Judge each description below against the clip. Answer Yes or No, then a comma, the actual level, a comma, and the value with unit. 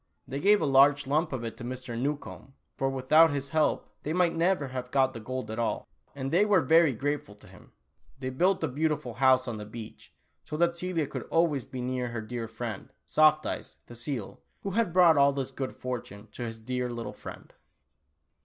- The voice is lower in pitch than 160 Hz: Yes, low, 135 Hz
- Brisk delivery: Yes, fast, 210 wpm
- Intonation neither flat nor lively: Yes, average, 4.2 semitones